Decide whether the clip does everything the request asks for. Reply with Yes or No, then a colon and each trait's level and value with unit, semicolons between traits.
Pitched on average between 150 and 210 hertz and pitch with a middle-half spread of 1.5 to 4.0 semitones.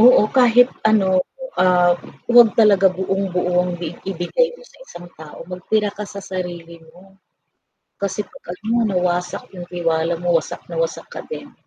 Yes: medium, 185 Hz; average, 3.3 semitones